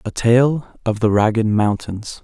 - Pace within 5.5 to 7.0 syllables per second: No, 4.1 syllables/s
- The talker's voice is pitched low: Yes, low, 115 Hz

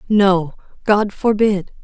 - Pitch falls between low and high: No, high, 200 Hz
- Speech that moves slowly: Yes, slow, 100 wpm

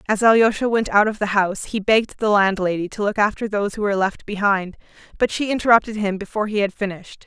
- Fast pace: Yes, fast, 225 wpm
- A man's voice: No, female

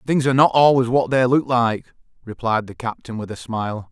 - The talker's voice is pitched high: No, low, 120 Hz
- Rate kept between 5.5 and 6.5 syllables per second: Yes, 5.6 syllables/s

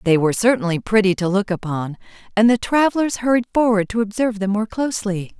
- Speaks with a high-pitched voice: Yes, high, 210 Hz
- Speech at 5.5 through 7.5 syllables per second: Yes, 6.2 syllables/s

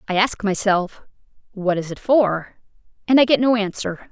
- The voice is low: No, high, 205 Hz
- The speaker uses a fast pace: No, average, 175 wpm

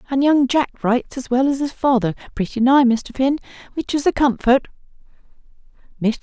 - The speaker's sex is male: No, female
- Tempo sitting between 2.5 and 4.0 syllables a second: No, 5.5 syllables/s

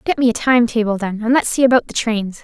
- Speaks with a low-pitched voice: No, high, 230 Hz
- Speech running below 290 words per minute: No, fast, 295 wpm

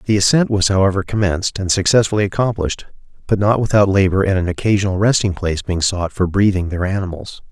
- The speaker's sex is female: No, male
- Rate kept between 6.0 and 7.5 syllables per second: Yes, 6.4 syllables/s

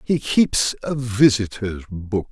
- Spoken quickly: No, slow, 130 wpm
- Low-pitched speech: Yes, low, 115 Hz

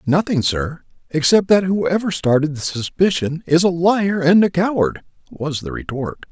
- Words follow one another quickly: No, average, 160 wpm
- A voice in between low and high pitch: Yes, medium, 165 Hz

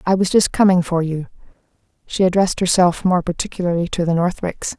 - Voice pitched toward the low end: No, medium, 180 Hz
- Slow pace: No, average, 175 wpm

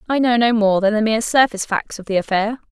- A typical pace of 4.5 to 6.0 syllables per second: No, 6.5 syllables/s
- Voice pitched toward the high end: Yes, high, 220 Hz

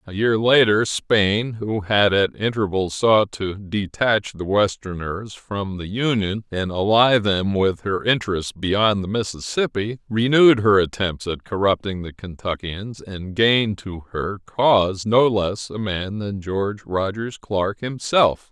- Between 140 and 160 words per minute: Yes, average, 150 wpm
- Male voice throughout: Yes, male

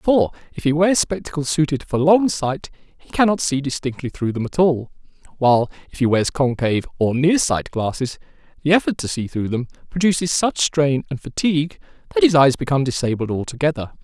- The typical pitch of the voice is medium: Yes, medium, 145 Hz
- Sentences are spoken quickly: No, average, 185 wpm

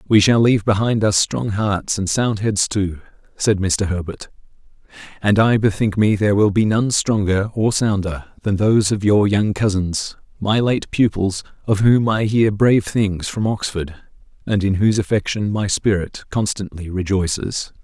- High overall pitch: No, low, 100 Hz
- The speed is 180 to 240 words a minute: No, average, 170 wpm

